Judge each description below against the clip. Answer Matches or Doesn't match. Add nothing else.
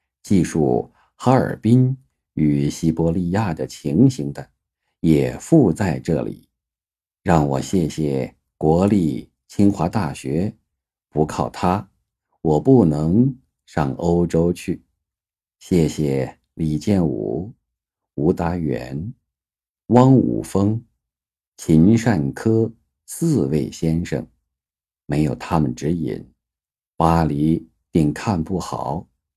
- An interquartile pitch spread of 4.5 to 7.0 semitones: Matches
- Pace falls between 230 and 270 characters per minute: Doesn't match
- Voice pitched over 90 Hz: Doesn't match